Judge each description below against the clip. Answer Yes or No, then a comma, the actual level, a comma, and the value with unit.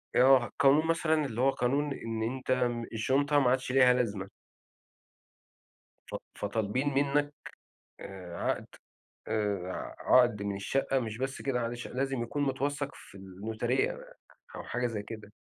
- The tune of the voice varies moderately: Yes, average, 3.8 semitones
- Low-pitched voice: Yes, low, 125 Hz